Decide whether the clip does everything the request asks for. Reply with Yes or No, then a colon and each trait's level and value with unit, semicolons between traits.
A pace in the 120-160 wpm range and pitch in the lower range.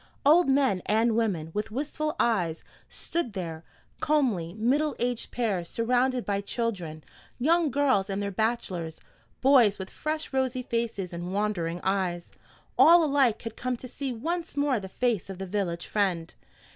No: average, 155 wpm; high, 225 Hz